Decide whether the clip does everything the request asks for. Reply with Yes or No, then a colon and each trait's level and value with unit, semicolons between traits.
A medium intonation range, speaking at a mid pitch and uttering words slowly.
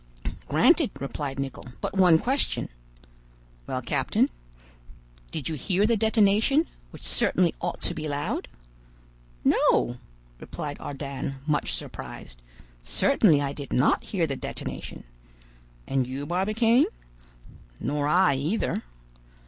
No: wide, 6.3 semitones; medium, 155 Hz; slow, 115 wpm